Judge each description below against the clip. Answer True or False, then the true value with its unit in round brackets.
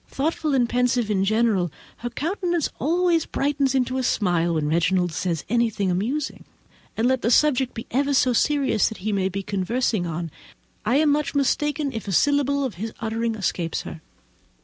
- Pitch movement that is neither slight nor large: False (6.4 semitones)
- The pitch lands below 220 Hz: False (235 Hz)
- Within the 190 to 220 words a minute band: False (175 wpm)